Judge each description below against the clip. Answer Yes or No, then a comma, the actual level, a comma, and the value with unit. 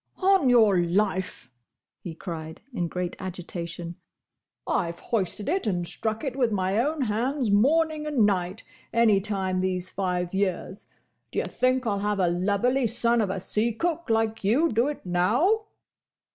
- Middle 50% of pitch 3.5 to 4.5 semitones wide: No, average, 5.2 semitones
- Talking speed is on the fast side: No, average, 160 wpm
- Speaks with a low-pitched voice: No, high, 210 Hz